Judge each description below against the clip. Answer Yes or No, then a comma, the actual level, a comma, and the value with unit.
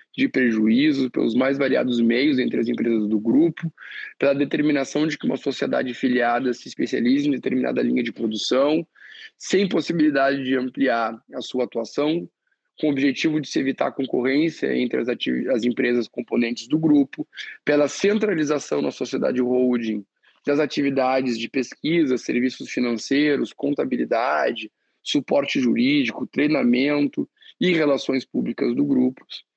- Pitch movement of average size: Yes, average, 4.2 semitones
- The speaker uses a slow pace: No, average, 135 wpm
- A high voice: No, low, 135 Hz